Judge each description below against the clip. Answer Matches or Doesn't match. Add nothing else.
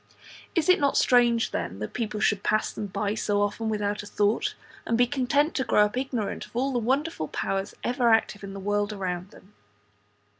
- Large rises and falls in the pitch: Doesn't match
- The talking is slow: Doesn't match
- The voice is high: Matches